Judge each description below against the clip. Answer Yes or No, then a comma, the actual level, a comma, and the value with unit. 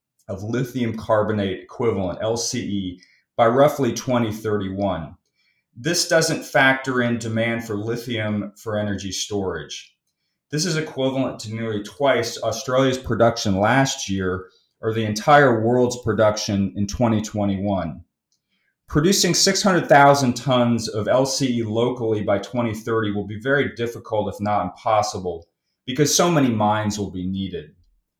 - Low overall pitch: Yes, low, 115 Hz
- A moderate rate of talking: No, slow, 120 wpm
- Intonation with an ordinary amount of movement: Yes, average, 3.8 semitones